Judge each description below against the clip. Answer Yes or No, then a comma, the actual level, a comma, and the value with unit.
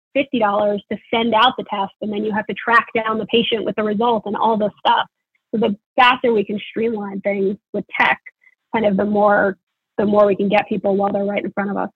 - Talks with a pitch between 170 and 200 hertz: No, high, 210 Hz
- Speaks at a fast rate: Yes, fast, 245 wpm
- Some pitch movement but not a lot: No, narrow, 2.1 semitones